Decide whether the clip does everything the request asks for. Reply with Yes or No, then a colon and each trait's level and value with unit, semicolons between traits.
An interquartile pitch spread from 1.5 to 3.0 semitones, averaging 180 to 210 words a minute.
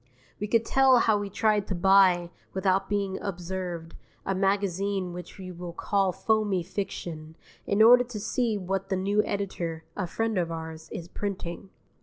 No: narrow, 2.6 semitones; average, 165 wpm